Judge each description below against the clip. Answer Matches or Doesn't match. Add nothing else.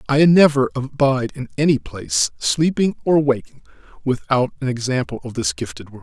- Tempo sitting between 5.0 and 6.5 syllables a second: Matches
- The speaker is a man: Matches